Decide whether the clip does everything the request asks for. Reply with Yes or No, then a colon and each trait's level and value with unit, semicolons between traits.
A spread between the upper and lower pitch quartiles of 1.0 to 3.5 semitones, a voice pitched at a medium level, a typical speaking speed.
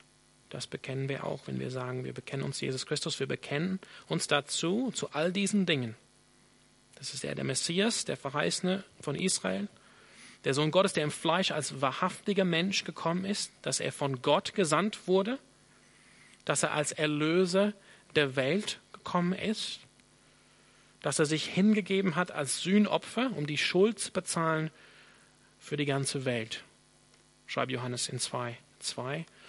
No: wide, 5.5 semitones; medium, 165 Hz; average, 150 wpm